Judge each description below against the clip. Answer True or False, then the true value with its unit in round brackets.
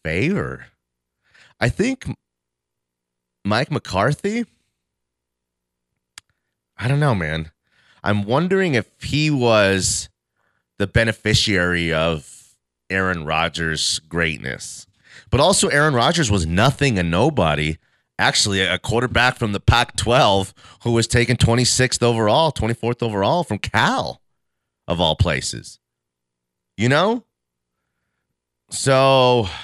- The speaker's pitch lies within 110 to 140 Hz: False (95 Hz)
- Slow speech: True (100 wpm)